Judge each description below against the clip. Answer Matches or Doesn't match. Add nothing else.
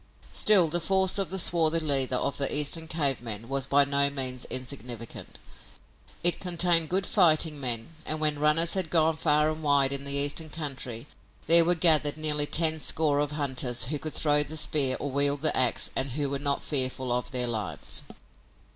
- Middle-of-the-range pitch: Matches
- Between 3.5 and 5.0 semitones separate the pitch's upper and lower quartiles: Doesn't match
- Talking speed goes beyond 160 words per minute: Matches